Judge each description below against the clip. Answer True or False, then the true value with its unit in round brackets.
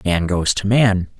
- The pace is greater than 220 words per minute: False (200 wpm)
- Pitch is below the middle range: True (100 Hz)